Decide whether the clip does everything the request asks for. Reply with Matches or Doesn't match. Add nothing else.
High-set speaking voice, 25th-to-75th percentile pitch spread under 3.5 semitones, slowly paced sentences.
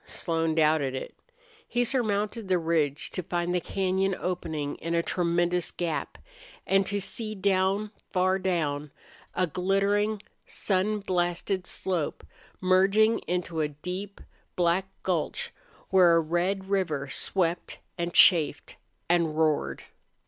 Doesn't match